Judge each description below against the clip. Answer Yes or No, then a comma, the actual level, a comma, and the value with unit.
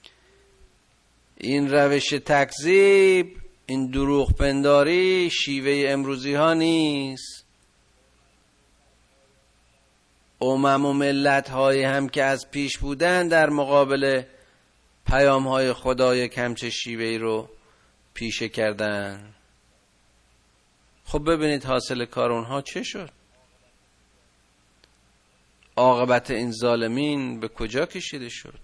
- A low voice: Yes, low, 130 Hz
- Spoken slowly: Yes, slow, 90 wpm